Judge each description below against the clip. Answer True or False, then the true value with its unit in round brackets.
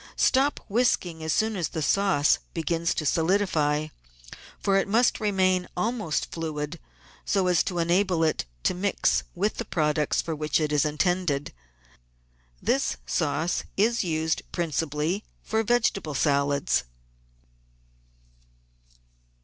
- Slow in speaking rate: True (120 wpm)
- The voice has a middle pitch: True (170 Hz)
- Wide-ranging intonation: False (4.4 semitones)